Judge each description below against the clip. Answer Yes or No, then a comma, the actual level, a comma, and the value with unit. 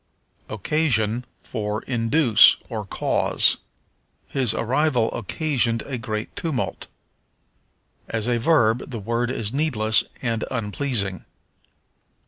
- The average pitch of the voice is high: No, low, 115 Hz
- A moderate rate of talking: No, slow, 100 wpm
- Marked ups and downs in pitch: No, average, 3.2 semitones